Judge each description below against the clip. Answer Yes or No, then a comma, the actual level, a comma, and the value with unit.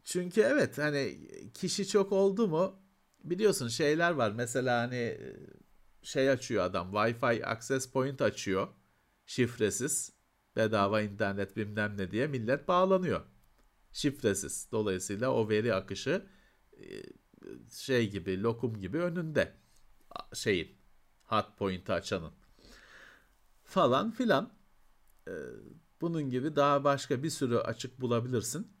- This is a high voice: No, low, 130 Hz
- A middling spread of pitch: No, wide, 7.0 semitones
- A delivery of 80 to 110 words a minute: Yes, average, 105 wpm